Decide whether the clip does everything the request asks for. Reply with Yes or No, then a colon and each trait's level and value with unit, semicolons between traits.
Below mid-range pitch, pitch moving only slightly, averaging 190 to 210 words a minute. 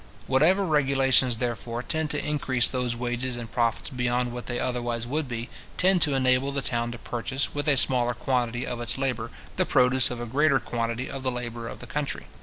Yes: low, 125 Hz; narrow, 2.2 semitones; fast, 205 wpm